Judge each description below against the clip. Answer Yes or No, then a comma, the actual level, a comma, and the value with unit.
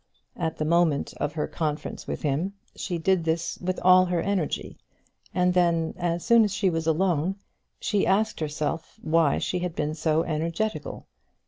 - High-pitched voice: No, medium, 170 Hz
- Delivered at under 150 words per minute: No, average, 165 wpm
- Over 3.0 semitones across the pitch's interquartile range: No, average, 2.7 semitones